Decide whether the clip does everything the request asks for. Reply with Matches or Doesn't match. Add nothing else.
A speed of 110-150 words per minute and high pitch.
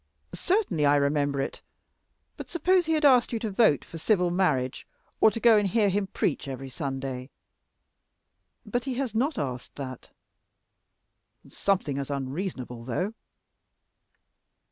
Doesn't match